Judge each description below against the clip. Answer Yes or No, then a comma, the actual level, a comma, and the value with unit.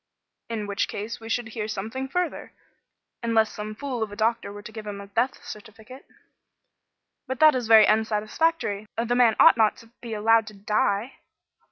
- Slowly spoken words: No, average, 175 wpm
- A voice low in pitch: No, high, 220 Hz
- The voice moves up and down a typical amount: No, narrow, 2.3 semitones